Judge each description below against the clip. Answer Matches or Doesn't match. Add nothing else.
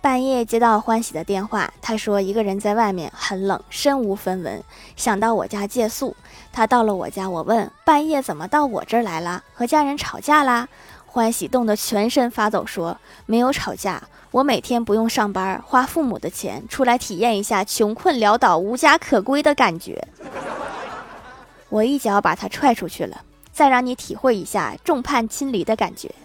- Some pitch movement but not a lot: Matches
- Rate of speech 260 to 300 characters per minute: Matches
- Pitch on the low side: Doesn't match